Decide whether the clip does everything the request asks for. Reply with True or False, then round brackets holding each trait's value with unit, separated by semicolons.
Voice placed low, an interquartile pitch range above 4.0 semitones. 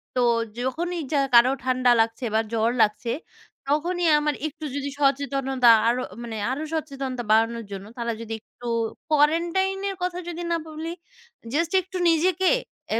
False (275 Hz; 5.4 semitones)